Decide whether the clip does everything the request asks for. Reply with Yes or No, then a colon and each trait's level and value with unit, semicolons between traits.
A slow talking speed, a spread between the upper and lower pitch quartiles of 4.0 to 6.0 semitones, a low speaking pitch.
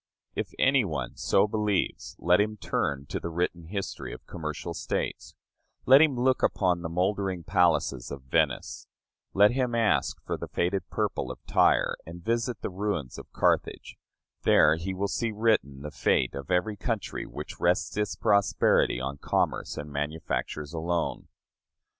No: average, 160 wpm; wide, 5.4 semitones; very low, 90 Hz